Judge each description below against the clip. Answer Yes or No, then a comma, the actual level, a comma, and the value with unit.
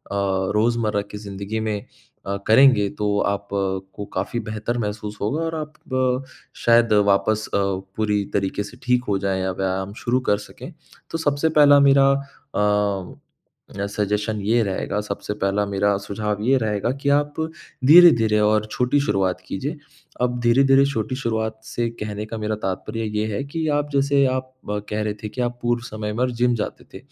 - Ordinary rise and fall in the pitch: Yes, average, 3.4 semitones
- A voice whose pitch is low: Yes, low, 110 Hz